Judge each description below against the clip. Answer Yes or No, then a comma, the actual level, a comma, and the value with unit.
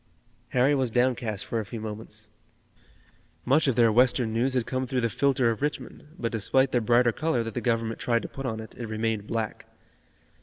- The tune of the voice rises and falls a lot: No, narrow, 2.5 semitones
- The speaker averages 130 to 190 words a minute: No, average, 200 wpm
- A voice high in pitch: No, low, 120 Hz